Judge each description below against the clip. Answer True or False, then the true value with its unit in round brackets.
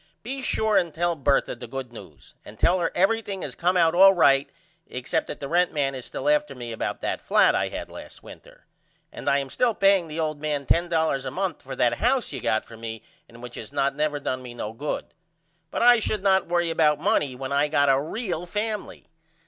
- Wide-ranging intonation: True (6.1 semitones)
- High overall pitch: False (155 Hz)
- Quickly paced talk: True (225 wpm)